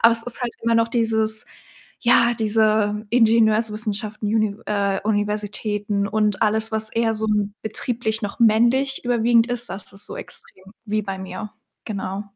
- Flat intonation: Yes, narrow, 1.7 semitones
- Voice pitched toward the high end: Yes, high, 220 Hz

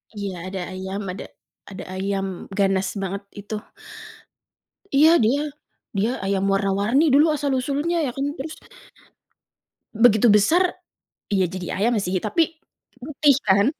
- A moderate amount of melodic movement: No, wide, 6.4 semitones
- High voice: Yes, high, 210 Hz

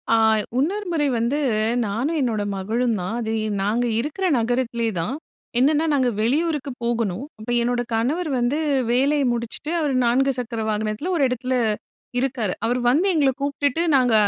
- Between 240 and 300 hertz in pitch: Yes, very high, 250 Hz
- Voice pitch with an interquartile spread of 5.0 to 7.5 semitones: No, average, 3.9 semitones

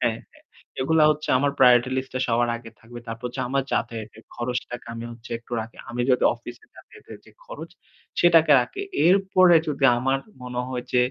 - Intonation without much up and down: No, average, 4.0 semitones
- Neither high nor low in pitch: No, low, 125 Hz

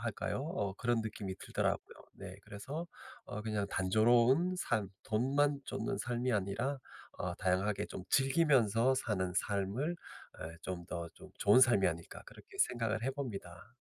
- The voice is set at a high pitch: No, low, 110 Hz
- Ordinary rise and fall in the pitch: Yes, average, 5.0 semitones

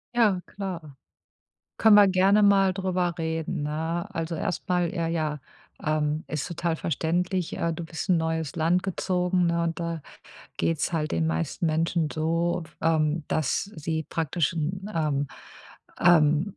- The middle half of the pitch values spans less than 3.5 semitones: Yes, narrow, 2.4 semitones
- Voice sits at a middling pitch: Yes, medium, 165 Hz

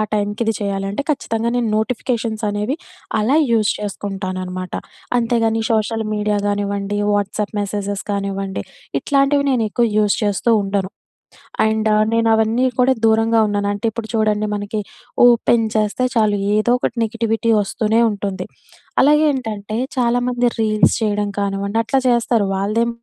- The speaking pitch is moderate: No, high, 215 Hz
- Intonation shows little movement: Yes, narrow, 2.2 semitones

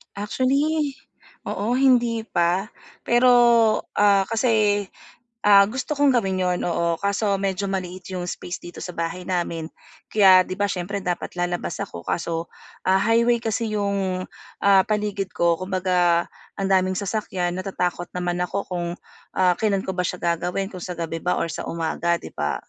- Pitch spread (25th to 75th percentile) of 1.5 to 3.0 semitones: Yes, average, 2.7 semitones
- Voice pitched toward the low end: No, high, 190 Hz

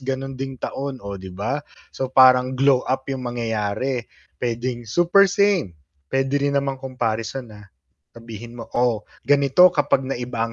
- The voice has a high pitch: No, low, 130 Hz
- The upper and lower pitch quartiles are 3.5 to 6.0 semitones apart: No, narrow, 2.6 semitones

